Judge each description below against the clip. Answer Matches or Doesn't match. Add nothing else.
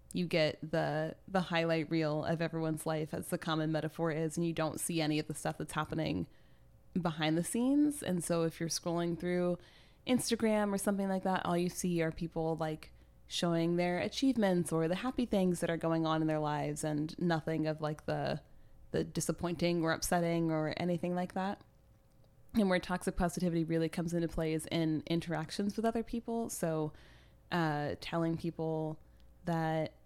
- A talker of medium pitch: Matches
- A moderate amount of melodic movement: Doesn't match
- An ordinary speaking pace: Matches